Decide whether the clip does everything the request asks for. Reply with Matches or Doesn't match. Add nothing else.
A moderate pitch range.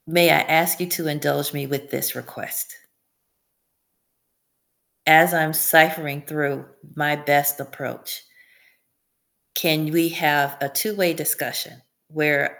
Doesn't match